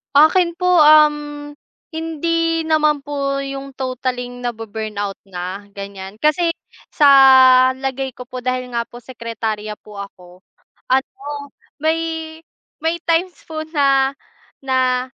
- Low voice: No, very high, 270 Hz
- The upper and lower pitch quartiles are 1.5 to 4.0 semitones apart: No, average, 4.7 semitones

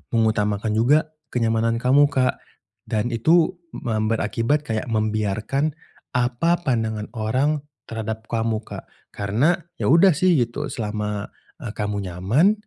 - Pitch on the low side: Yes, low, 115 Hz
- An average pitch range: Yes, average, 4.0 semitones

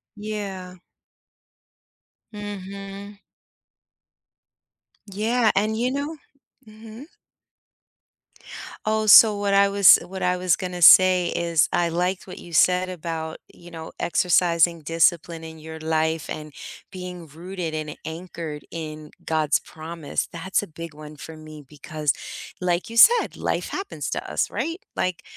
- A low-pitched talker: No, medium, 180 Hz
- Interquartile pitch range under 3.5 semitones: No, average, 3.8 semitones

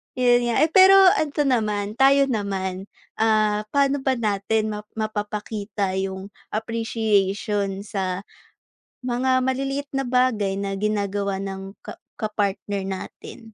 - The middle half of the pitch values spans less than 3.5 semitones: No, average, 4.0 semitones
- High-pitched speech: Yes, high, 215 Hz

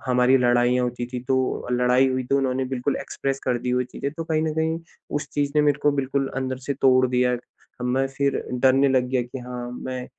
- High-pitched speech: No, low, 130 Hz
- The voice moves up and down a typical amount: No, narrow, 1.6 semitones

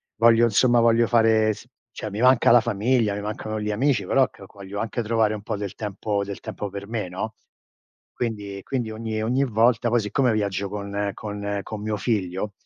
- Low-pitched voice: Yes, low, 110 Hz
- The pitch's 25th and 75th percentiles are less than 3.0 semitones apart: Yes, narrow, 2.4 semitones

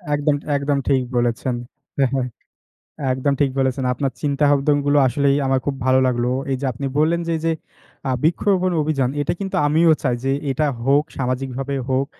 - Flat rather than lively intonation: Yes, narrow, 2.1 semitones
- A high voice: No, medium, 140 Hz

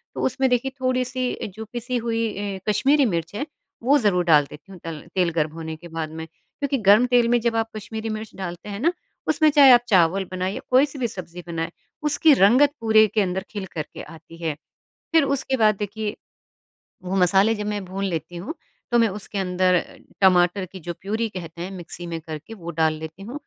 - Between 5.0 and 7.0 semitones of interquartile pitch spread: Yes, wide, 5.4 semitones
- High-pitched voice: Yes, high, 200 Hz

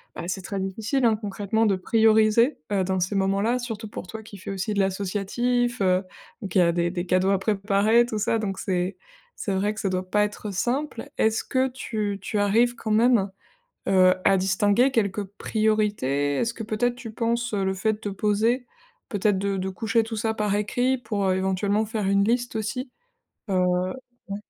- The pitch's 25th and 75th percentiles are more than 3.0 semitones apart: No, average, 2.7 semitones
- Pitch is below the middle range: No, high, 210 Hz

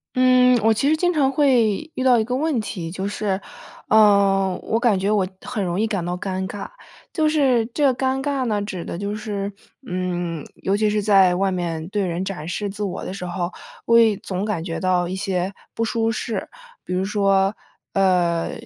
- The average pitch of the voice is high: Yes, high, 200 Hz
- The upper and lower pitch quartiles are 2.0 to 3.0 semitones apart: No, average, 3.9 semitones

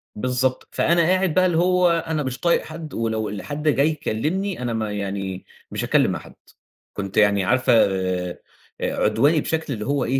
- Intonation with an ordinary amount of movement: No, wide, 7.4 semitones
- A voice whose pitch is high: No, low, 130 Hz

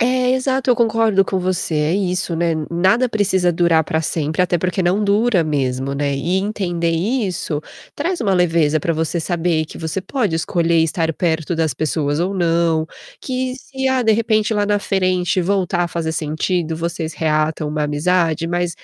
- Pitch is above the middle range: No, medium, 175 Hz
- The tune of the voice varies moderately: Yes, average, 3.9 semitones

